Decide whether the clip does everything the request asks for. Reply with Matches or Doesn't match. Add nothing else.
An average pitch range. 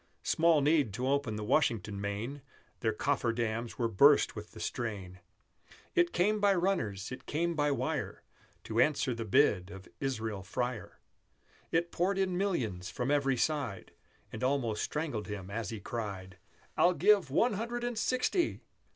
Doesn't match